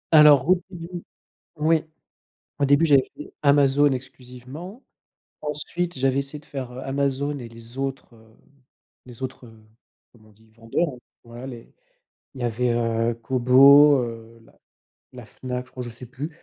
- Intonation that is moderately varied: Yes, average, 3.4 semitones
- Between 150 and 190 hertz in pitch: No, low, 130 Hz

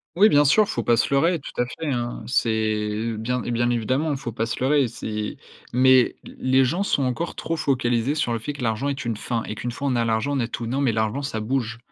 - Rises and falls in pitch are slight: No, average, 3.5 semitones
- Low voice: Yes, low, 125 Hz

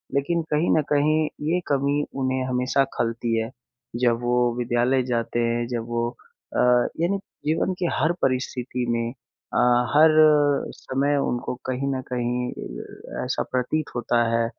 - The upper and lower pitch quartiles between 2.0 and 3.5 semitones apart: Yes, average, 3.1 semitones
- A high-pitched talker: No, low, 125 Hz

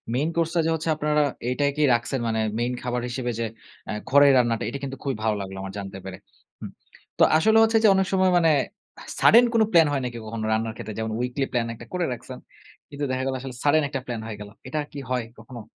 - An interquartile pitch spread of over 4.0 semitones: Yes, average, 4.9 semitones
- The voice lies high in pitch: No, low, 130 Hz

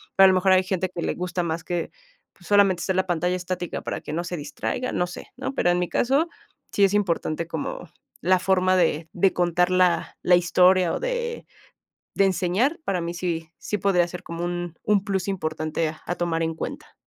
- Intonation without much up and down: Yes, narrow, 1.9 semitones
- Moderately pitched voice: Yes, medium, 180 Hz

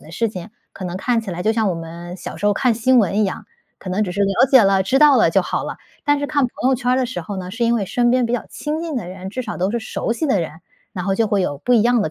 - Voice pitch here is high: Yes, high, 215 Hz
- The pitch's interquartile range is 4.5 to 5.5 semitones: Yes, average, 4.9 semitones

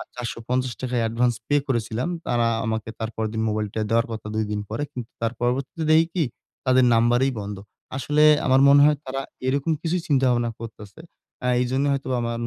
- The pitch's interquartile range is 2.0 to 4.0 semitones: Yes, average, 3.0 semitones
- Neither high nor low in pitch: No, low, 120 Hz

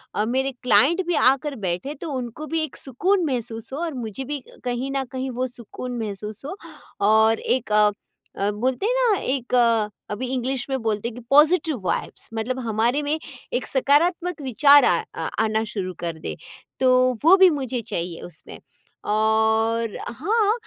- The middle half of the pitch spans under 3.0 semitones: No, average, 4.8 semitones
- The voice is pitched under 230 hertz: No, very high, 255 Hz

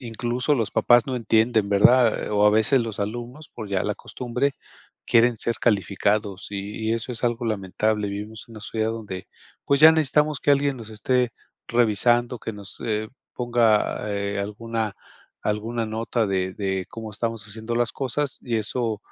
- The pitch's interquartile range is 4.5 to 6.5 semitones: No, narrow, 2.5 semitones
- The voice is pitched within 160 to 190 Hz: No, low, 115 Hz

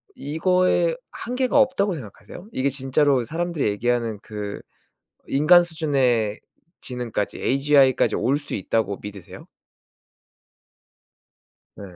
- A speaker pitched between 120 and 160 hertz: Yes, low, 135 Hz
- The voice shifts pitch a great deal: Yes, wide, 6.7 semitones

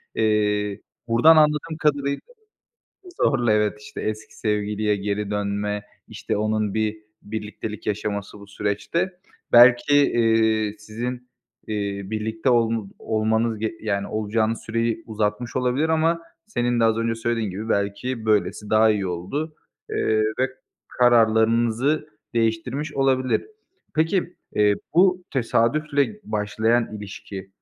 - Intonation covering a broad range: No, average, 3.0 semitones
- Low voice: Yes, low, 110 Hz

